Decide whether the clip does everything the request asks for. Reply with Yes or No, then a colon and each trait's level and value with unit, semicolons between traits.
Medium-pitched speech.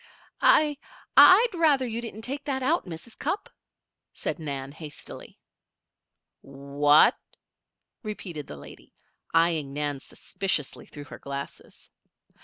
Yes: medium, 165 Hz